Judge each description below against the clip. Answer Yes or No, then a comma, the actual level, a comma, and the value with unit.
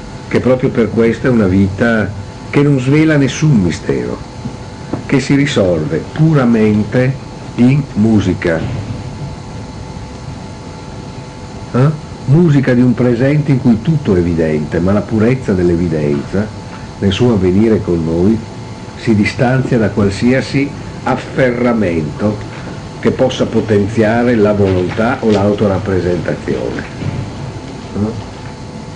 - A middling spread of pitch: Yes, average, 3.8 semitones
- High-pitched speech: No, low, 120 Hz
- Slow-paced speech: Yes, slow, 105 wpm